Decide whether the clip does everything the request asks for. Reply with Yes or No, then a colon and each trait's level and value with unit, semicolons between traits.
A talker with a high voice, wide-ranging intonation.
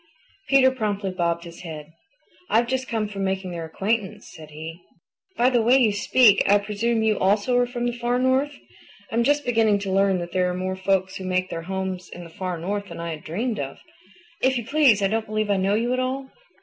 No: high, 205 Hz; average, 4.6 semitones